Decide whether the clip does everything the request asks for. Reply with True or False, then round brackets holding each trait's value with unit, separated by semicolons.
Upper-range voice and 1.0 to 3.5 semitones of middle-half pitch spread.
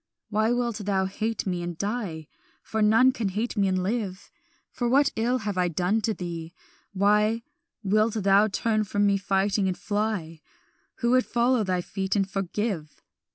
True (205 Hz; 2.8 semitones)